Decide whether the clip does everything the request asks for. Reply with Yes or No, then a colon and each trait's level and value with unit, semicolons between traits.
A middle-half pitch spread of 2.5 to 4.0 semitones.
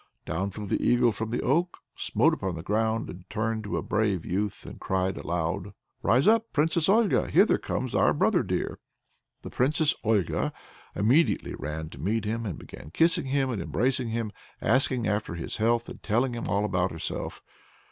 No: average, 5.3 semitones